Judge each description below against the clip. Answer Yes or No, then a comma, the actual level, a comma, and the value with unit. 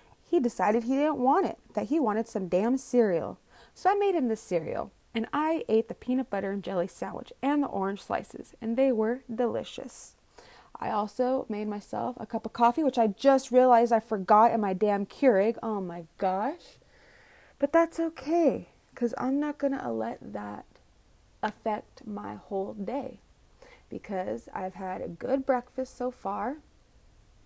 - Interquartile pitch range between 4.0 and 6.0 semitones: Yes, average, 4.5 semitones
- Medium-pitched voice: No, high, 235 Hz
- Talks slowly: No, average, 170 wpm